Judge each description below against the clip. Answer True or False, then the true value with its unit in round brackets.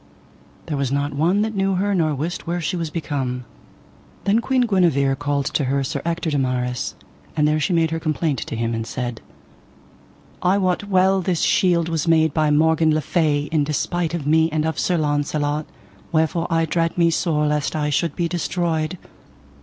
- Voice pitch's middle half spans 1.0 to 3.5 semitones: True (2.9 semitones)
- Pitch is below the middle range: False (160 Hz)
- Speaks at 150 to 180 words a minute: False (190 wpm)